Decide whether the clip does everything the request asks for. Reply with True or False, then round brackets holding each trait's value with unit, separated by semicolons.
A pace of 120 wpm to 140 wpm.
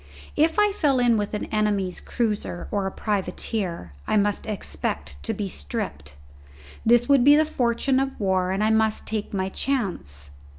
False (170 wpm)